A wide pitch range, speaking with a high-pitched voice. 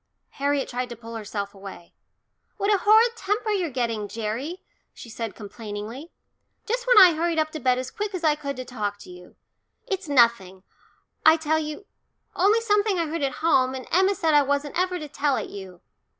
Yes: wide, 7.9 semitones; very high, 290 Hz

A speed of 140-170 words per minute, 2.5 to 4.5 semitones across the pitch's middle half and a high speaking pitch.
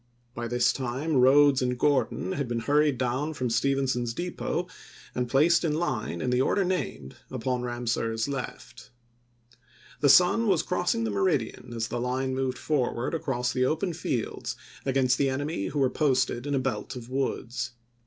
No: average, 165 wpm; average, 3.1 semitones; low, 130 Hz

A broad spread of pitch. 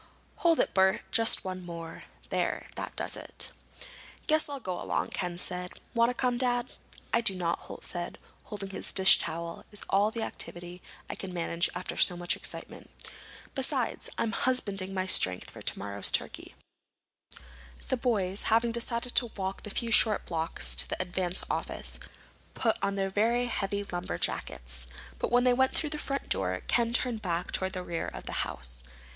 No: average, 5.0 semitones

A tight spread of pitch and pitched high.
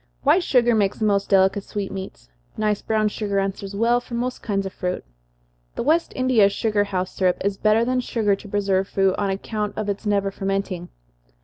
Yes: narrow, 2.2 semitones; high, 205 Hz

